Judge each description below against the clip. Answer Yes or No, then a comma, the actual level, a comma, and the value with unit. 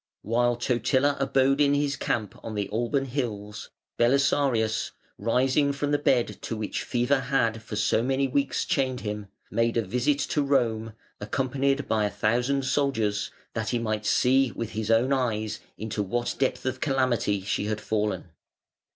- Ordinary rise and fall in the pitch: Yes, average, 3.8 semitones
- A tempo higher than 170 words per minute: No, average, 160 wpm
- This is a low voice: Yes, low, 120 Hz